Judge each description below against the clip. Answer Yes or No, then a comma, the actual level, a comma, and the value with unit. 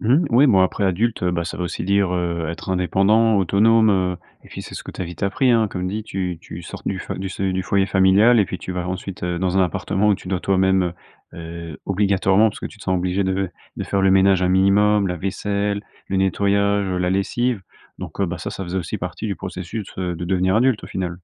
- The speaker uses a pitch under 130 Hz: Yes, very low, 95 Hz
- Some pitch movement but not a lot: No, narrow, 1.9 semitones